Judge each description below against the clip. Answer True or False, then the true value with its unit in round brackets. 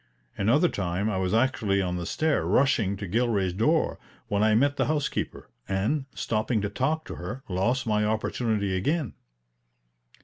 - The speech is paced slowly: False (160 wpm)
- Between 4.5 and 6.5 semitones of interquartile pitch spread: True (5.2 semitones)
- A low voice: True (110 Hz)